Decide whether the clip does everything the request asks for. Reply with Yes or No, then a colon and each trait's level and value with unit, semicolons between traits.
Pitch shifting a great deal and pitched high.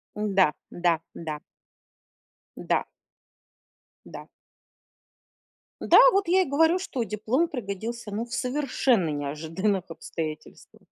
Yes: wide, 7.8 semitones; high, 210 Hz